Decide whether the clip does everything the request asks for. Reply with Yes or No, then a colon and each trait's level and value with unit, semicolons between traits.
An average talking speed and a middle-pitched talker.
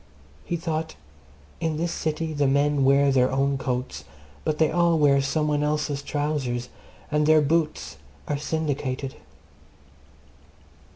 No: slow, 130 wpm; medium, 145 Hz